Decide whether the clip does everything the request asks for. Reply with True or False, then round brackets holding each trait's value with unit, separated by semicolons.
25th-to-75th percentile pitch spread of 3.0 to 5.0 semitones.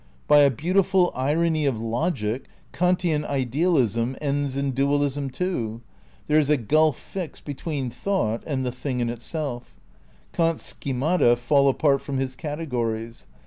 True (4.1 semitones)